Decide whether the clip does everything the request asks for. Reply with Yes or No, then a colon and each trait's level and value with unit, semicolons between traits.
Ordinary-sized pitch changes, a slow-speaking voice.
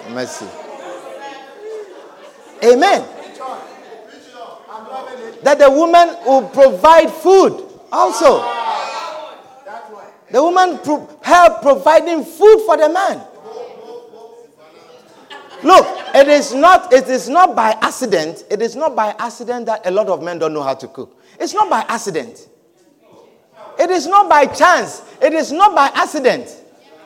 No: wide, 6.3 semitones; slow, 125 wpm